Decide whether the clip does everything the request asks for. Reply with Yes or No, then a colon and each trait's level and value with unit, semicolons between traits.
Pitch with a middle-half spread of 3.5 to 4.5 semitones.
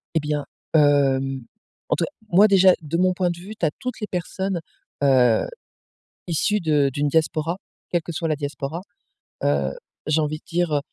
Yes: average, 3.8 semitones